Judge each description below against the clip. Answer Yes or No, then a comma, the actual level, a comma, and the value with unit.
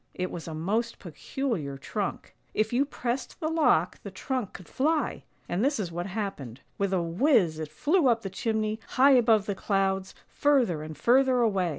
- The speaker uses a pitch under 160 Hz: No, high, 215 Hz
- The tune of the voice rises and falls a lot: Yes, wide, 6.4 semitones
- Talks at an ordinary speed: Yes, average, 185 wpm